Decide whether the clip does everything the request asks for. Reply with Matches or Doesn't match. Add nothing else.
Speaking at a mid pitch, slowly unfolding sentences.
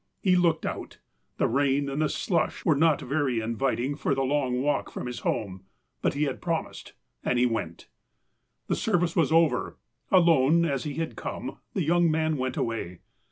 Doesn't match